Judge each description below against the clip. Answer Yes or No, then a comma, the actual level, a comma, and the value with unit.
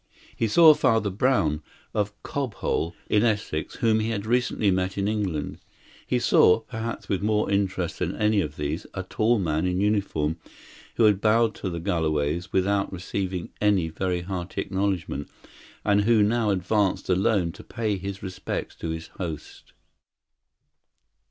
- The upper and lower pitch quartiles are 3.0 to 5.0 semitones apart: Yes, average, 3.4 semitones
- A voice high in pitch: No, low, 100 Hz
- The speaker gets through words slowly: No, average, 150 wpm